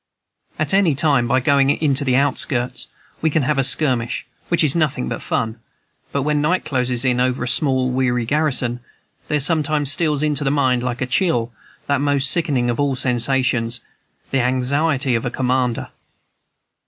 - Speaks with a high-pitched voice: No, low, 135 Hz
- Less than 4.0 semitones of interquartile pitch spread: Yes, average, 2.9 semitones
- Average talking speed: Yes, average, 175 wpm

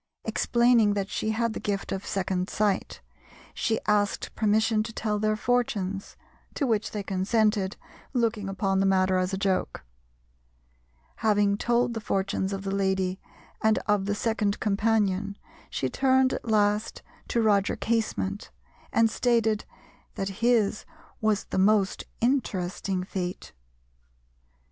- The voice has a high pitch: Yes, high, 205 Hz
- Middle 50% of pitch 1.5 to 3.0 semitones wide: Yes, narrow, 2.4 semitones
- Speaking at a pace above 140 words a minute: No, slow, 135 wpm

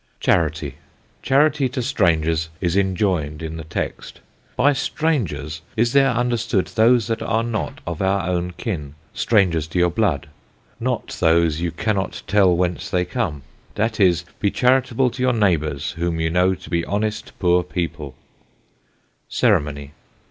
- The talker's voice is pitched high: No, very low, 90 Hz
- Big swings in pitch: Yes, wide, 5.7 semitones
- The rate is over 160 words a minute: No, average, 150 wpm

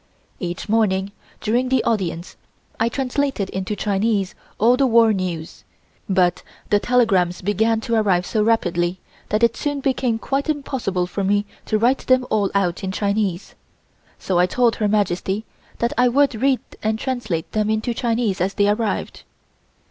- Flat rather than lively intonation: No, average, 3.8 semitones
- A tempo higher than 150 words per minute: Yes, average, 160 wpm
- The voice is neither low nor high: No, high, 215 Hz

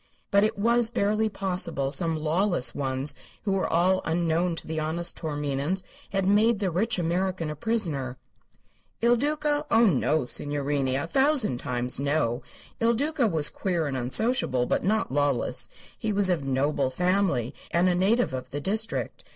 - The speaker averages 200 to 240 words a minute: No, average, 160 wpm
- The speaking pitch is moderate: Yes, medium, 175 Hz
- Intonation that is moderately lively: No, wide, 6.5 semitones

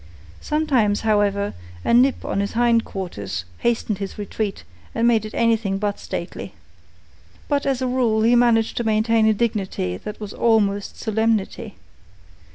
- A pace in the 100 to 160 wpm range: Yes, average, 150 wpm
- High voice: Yes, high, 220 Hz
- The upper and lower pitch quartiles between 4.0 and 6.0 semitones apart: No, average, 2.7 semitones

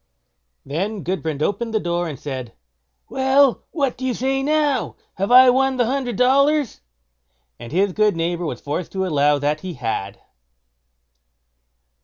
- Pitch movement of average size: No, wide, 8.9 semitones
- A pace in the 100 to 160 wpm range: Yes, average, 145 wpm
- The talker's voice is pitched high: Yes, high, 200 Hz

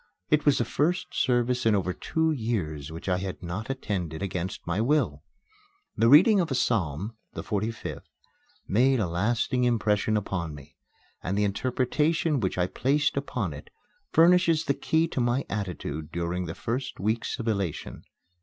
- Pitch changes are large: Yes, wide, 6.8 semitones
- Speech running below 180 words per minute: Yes, average, 165 wpm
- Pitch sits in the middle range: No, low, 110 Hz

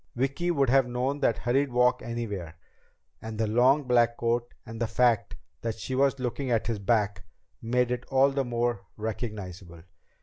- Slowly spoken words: No, average, 170 wpm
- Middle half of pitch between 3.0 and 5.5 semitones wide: No, narrow, 2.6 semitones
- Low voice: Yes, low, 120 Hz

